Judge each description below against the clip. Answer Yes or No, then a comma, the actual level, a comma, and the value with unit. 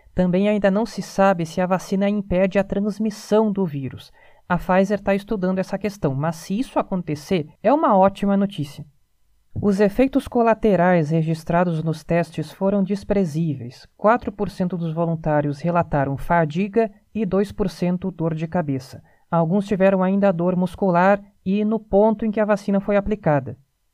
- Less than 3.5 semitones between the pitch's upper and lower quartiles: No, average, 3.9 semitones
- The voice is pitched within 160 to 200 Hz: Yes, high, 190 Hz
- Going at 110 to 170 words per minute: Yes, average, 150 wpm